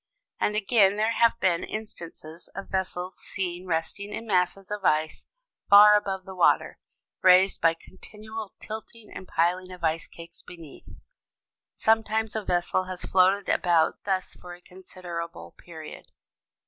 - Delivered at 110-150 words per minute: Yes, average, 140 wpm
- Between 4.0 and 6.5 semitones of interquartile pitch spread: No, average, 3.1 semitones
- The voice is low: No, medium, 185 Hz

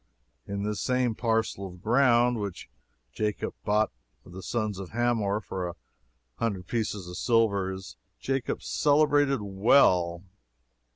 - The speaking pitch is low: Yes, low, 105 Hz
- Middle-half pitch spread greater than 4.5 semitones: No, average, 4.0 semitones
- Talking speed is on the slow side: Yes, slow, 130 wpm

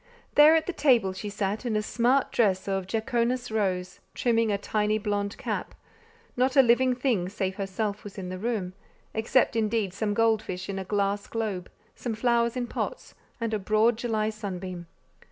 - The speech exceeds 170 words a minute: Yes, average, 180 wpm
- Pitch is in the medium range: No, high, 215 Hz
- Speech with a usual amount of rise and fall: Yes, average, 3.2 semitones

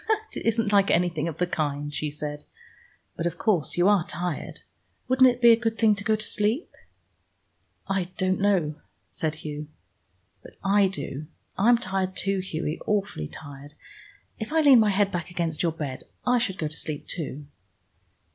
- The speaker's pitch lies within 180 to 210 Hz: Yes, medium, 185 Hz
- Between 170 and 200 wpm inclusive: Yes, average, 175 wpm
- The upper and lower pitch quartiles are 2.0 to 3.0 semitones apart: No, wide, 5.4 semitones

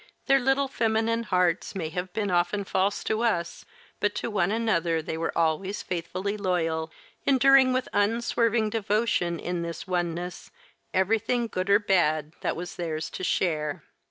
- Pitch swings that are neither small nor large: Yes, average, 4.6 semitones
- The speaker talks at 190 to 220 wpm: No, average, 155 wpm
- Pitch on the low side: No, high, 190 Hz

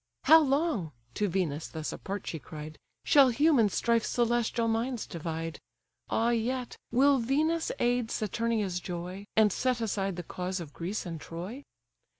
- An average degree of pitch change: No, wide, 5.8 semitones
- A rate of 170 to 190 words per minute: No, average, 150 wpm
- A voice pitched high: Yes, high, 220 Hz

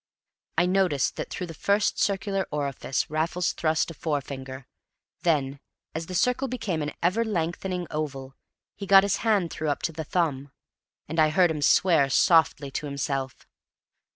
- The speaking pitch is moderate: Yes, medium, 160 Hz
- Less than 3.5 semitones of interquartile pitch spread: No, average, 4.5 semitones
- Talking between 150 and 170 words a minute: Yes, average, 160 wpm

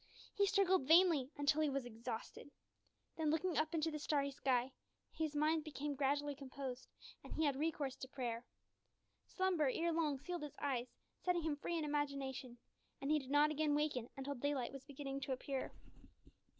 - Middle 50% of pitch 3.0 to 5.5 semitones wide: No, narrow, 2.6 semitones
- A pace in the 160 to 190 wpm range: Yes, average, 175 wpm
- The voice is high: Yes, very high, 290 Hz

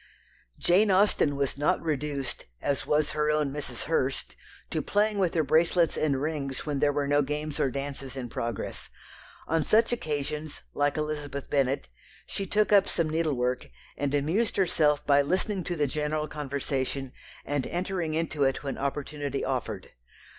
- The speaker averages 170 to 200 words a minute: No, average, 160 wpm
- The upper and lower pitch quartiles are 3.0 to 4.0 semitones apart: No, narrow, 2.6 semitones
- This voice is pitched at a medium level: Yes, medium, 150 Hz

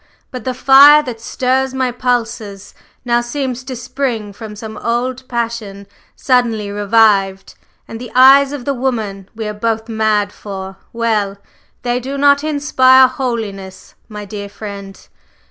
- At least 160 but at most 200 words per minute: No, average, 145 wpm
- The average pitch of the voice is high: Yes, high, 235 Hz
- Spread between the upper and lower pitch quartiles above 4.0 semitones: No, average, 3.7 semitones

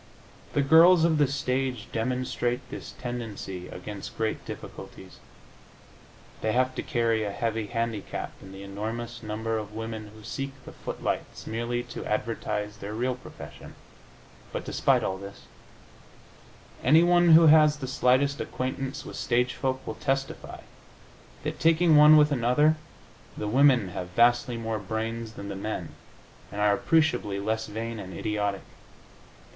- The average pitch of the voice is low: Yes, low, 115 Hz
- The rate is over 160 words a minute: No, average, 140 wpm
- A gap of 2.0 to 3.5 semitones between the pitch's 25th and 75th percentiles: No, average, 4.1 semitones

